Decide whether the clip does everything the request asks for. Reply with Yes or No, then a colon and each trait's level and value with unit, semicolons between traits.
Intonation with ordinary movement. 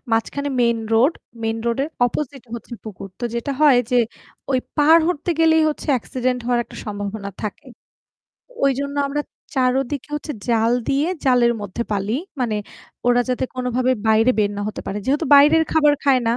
Yes: average, 4.0 semitones